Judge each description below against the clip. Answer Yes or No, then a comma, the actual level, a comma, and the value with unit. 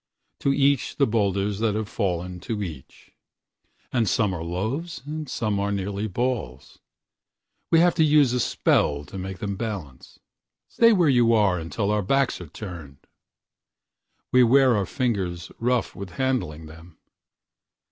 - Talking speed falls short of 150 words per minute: Yes, slow, 135 wpm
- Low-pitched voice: Yes, low, 105 Hz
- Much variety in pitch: Yes, wide, 5.8 semitones